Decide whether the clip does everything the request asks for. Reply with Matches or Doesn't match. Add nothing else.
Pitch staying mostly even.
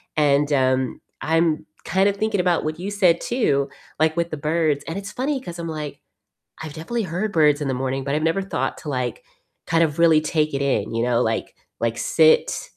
Doesn't match